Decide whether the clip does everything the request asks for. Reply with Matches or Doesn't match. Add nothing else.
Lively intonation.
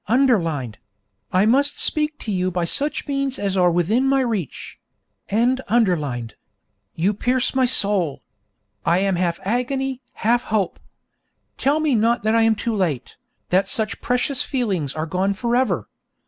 Matches